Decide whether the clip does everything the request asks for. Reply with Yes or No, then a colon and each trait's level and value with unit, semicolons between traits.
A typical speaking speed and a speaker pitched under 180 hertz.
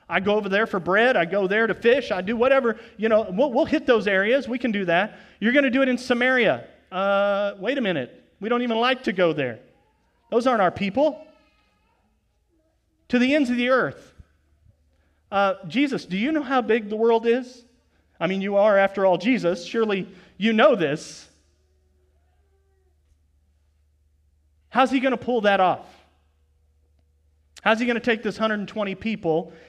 No: average, 180 wpm; high, 200 Hz